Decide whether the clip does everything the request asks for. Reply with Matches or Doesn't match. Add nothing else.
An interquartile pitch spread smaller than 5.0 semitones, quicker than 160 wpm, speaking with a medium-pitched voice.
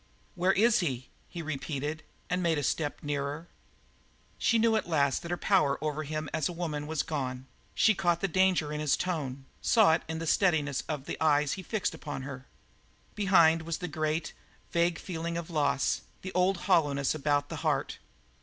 Matches